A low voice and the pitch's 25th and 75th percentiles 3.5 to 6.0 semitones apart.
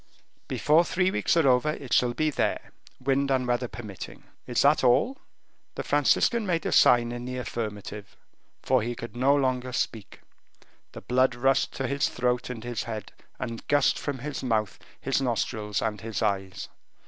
No: low, 125 Hz; average, 3.1 semitones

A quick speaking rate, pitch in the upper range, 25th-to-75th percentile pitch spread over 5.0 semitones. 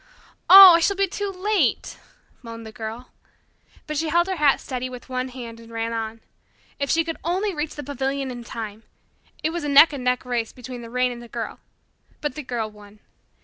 Yes: fast, 210 wpm; very high, 255 Hz; wide, 5.6 semitones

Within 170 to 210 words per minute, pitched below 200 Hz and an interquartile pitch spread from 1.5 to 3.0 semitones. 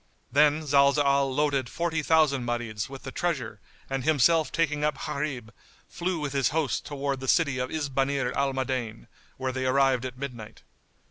No: average, 160 wpm; medium, 140 Hz; narrow, 2.6 semitones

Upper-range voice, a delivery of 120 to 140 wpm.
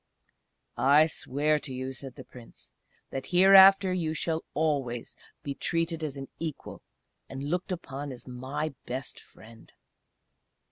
No: medium, 145 Hz; slow, 135 wpm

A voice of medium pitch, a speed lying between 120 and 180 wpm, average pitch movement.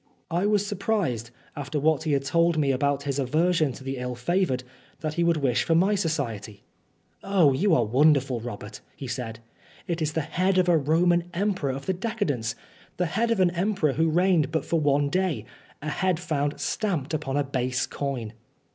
No: medium, 155 Hz; average, 190 wpm; average, 4.8 semitones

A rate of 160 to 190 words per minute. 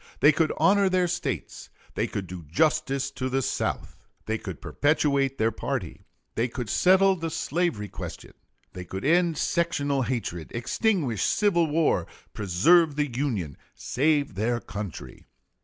No: average, 140 wpm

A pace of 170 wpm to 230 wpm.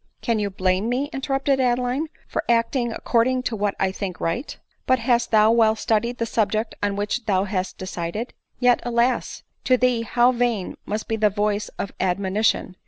Yes: average, 200 wpm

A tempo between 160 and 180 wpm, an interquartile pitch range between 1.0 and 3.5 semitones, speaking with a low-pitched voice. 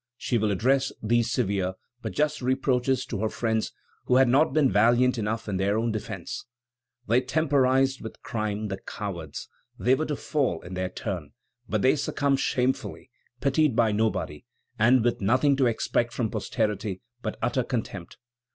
No: average, 165 wpm; average, 3.9 semitones; low, 120 Hz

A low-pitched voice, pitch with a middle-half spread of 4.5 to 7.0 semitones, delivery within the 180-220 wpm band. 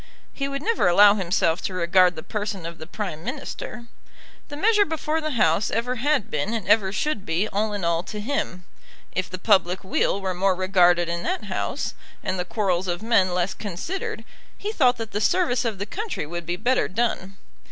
No: high, 200 Hz; average, 5.3 semitones; average, 200 wpm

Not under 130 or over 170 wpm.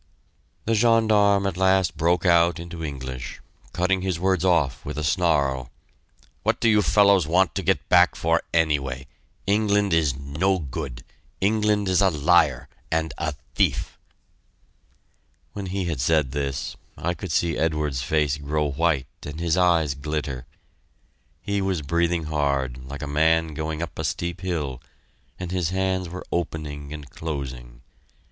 Yes: average, 150 wpm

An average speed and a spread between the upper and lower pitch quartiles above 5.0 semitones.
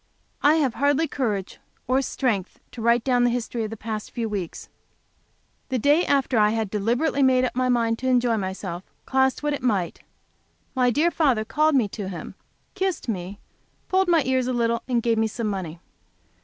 No: average, 190 wpm; average, 3.6 semitones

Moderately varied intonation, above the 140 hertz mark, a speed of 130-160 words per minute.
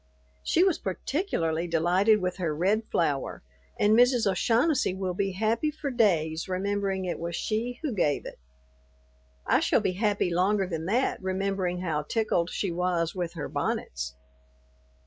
Yes: average, 4.1 semitones; high, 190 Hz; average, 150 wpm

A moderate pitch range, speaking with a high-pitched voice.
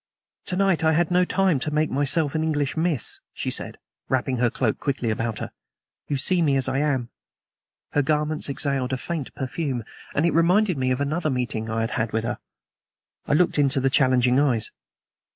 No: average, 3.8 semitones; medium, 140 Hz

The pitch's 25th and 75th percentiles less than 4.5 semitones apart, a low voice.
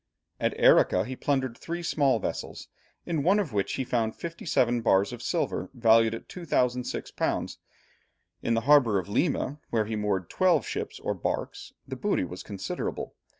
No: average, 5.2 semitones; low, 120 Hz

